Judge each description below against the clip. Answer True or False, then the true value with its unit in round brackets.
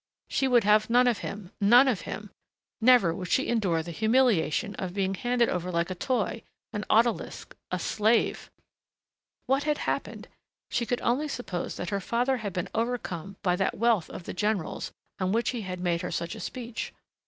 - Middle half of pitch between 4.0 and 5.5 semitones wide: True (4.7 semitones)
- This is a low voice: False (215 Hz)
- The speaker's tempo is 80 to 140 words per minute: False (190 wpm)